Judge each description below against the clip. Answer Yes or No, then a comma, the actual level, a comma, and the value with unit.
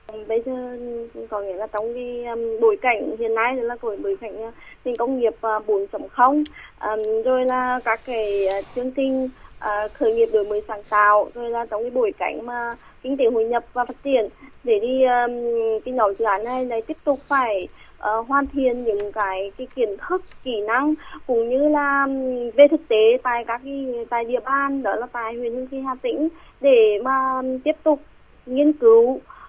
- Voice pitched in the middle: No, high, 245 Hz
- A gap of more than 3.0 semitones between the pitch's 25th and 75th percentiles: Yes, average, 3.4 semitones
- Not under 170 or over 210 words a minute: Yes, average, 205 wpm